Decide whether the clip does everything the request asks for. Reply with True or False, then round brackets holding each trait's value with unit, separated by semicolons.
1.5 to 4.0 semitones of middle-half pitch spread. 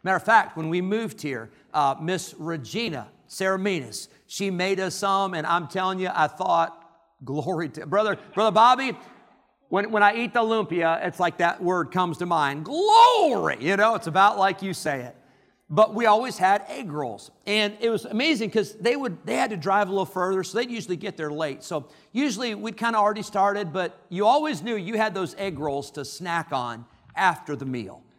False (4.4 semitones)